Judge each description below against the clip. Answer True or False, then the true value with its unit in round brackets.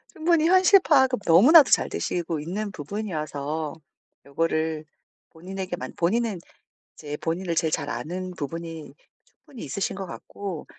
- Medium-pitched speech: True (175 Hz)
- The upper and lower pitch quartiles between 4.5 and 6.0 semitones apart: True (5.2 semitones)